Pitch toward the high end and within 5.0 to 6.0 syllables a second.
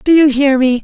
Yes: very high, 275 Hz; 5.1 syllables/s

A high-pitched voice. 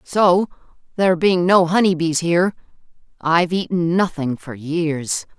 No: medium, 170 Hz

